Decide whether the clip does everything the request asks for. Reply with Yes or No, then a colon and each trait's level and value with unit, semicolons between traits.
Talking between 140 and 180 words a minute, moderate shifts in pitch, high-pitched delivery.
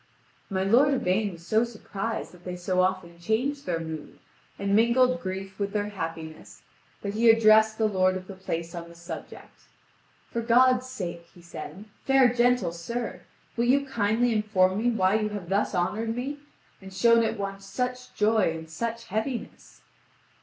Yes: average, 170 wpm; average, 4.1 semitones; high, 210 Hz